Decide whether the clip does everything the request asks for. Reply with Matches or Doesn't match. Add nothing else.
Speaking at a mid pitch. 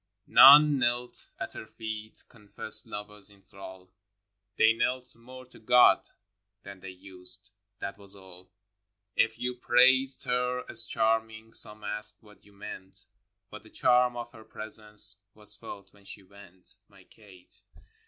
Doesn't match